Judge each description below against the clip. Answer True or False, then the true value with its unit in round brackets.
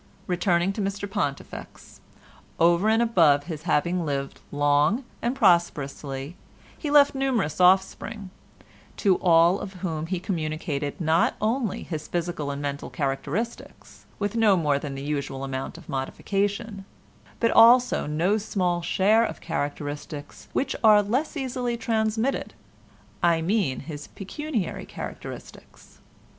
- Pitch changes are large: True (6.6 semitones)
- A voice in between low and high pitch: True (175 Hz)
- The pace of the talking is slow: True (125 wpm)